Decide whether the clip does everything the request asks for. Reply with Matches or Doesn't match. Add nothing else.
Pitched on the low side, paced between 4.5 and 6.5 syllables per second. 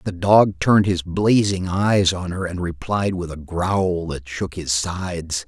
Doesn't match